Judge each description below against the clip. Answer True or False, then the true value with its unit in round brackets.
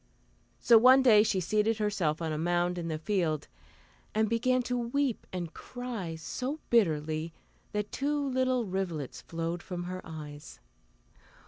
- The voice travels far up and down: True (6.4 semitones)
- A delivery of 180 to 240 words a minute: False (145 wpm)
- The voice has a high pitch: True (195 Hz)